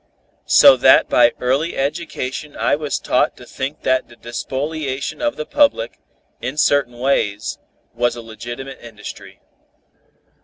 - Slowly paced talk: Yes, slow, 130 wpm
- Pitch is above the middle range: No, low, 135 Hz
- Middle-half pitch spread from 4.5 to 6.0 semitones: No, average, 4.0 semitones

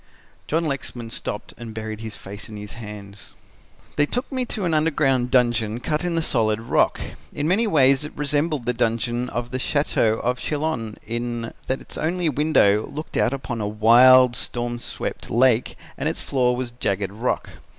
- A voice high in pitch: No, low, 125 Hz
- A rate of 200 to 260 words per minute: No, average, 180 wpm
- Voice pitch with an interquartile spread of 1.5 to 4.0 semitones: No, average, 4.6 semitones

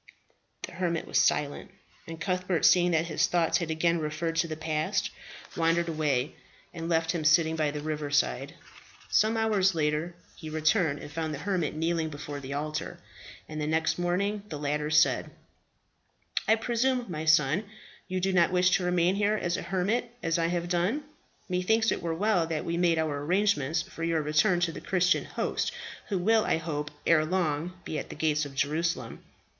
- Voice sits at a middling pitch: Yes, medium, 165 Hz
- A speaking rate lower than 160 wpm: No, average, 185 wpm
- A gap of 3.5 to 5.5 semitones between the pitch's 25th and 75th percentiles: No, average, 2.8 semitones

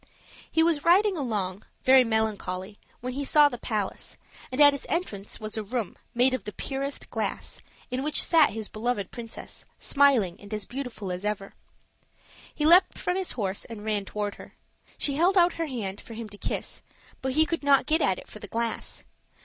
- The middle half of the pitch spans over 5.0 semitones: Yes, wide, 5.5 semitones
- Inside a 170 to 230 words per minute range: Yes, average, 190 wpm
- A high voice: Yes, high, 240 Hz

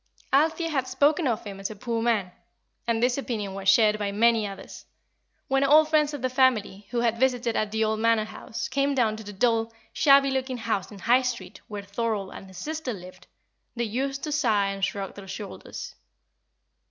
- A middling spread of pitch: Yes, average, 4.3 semitones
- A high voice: Yes, high, 230 Hz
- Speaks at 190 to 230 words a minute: Yes, average, 200 wpm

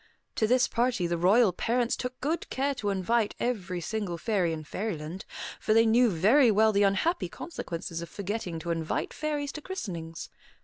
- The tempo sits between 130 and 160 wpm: No, average, 175 wpm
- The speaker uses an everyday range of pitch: No, wide, 6.0 semitones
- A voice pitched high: Yes, high, 215 Hz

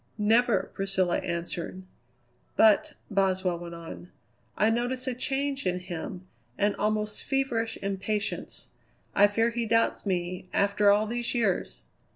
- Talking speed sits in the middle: No, slow, 130 wpm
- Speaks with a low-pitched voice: No, high, 210 Hz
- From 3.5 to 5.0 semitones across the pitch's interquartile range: Yes, average, 3.8 semitones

